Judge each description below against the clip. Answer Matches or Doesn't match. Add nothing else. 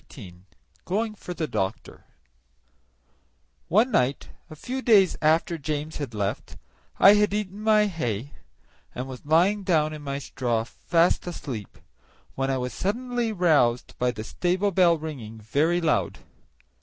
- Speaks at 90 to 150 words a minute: Matches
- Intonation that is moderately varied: Doesn't match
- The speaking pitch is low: Doesn't match